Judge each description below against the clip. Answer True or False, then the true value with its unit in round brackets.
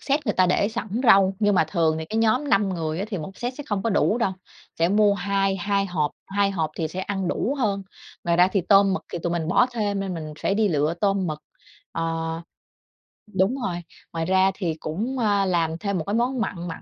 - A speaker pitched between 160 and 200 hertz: True (195 Hz)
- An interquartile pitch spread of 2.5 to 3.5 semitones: True (3.2 semitones)